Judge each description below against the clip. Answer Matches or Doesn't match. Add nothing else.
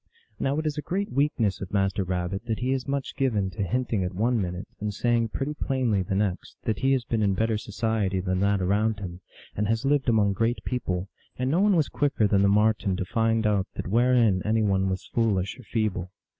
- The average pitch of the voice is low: Matches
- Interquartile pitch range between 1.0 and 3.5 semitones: Doesn't match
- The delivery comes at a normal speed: Doesn't match